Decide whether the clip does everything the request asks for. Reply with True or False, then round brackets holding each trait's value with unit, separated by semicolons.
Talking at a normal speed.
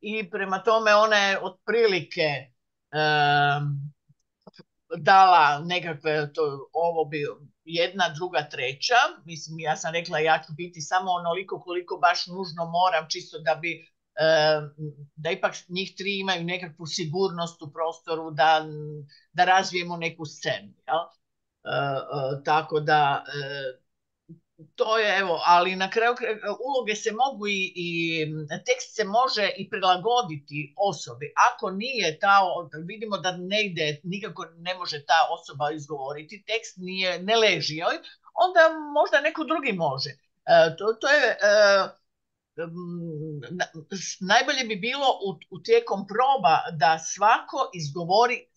True (130 wpm)